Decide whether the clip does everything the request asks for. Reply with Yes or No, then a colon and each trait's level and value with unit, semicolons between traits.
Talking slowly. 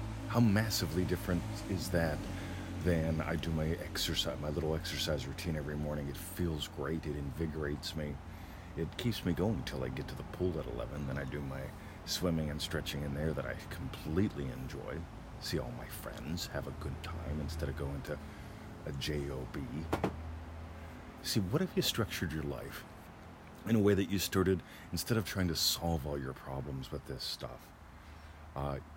No: average, 180 wpm